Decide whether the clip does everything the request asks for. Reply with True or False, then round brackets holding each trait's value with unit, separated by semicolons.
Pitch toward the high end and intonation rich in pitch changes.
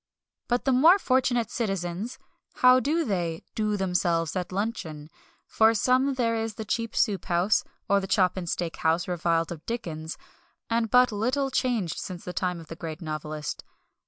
True (200 Hz; 5.8 semitones)